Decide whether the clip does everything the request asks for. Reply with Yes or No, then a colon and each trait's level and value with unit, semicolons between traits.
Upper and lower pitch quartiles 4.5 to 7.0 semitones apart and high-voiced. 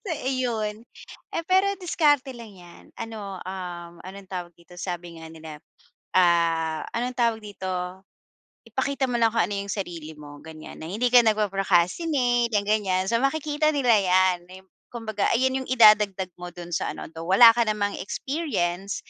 Yes: average, 5.3 semitones; high, 205 Hz